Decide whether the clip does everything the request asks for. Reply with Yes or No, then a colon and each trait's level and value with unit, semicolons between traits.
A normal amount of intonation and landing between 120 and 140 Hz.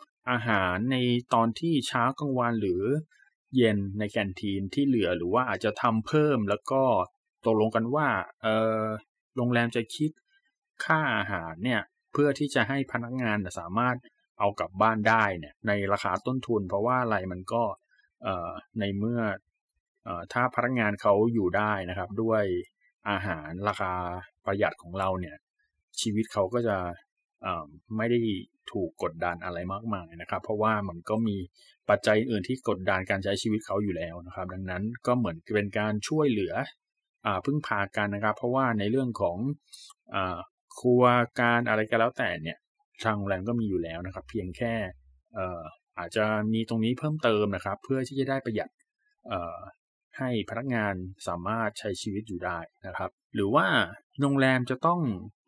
No: average, 4.1 semitones; low, 110 Hz